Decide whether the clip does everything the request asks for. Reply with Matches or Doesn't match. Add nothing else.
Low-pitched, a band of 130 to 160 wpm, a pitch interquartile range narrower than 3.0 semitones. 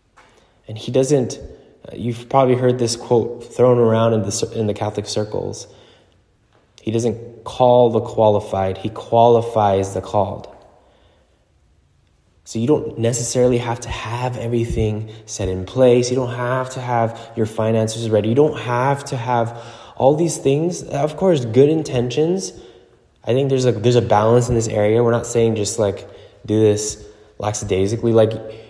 Matches